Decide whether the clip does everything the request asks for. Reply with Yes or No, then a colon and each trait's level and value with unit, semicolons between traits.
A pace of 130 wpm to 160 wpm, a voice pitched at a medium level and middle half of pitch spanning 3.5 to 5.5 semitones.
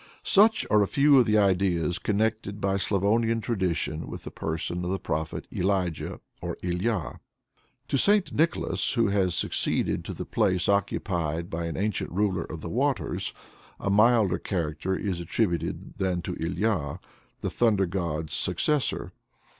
No: average, 150 wpm; very low, 95 Hz; average, 4.1 semitones